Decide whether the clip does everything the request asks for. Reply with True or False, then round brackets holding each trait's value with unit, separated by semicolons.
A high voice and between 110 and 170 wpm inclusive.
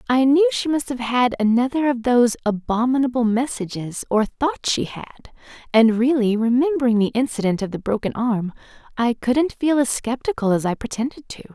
True (245 Hz; 160 wpm)